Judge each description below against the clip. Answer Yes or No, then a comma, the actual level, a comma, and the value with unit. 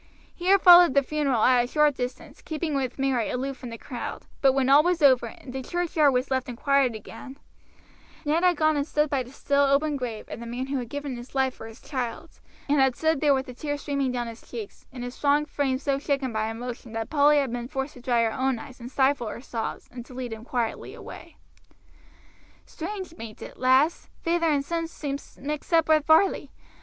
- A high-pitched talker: Yes, very high, 270 Hz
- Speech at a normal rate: No, fast, 225 wpm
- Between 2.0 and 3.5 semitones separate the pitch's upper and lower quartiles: Yes, average, 3.2 semitones